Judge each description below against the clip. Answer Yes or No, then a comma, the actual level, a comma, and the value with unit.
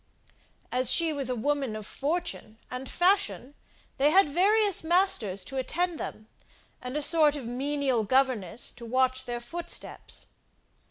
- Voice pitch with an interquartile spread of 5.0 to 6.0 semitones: Yes, average, 5.3 semitones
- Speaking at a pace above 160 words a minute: No, average, 145 wpm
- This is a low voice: No, very high, 270 Hz